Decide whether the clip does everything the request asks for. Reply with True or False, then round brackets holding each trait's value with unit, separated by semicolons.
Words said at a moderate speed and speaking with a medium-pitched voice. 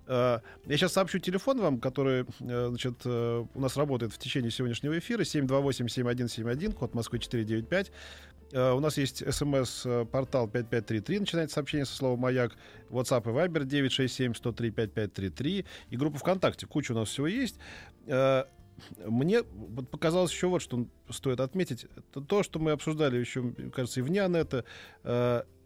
False (150 wpm; 130 Hz)